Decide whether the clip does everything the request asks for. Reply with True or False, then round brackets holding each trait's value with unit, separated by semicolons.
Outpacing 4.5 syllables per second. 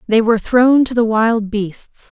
False (4.1 syllables/s)